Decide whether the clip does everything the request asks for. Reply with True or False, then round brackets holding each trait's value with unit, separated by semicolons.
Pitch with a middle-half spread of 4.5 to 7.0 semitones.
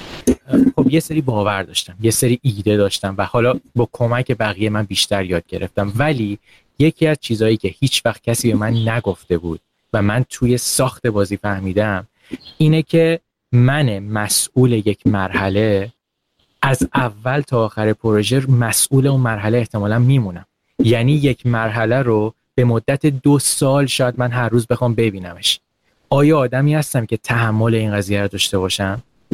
False (4.0 semitones)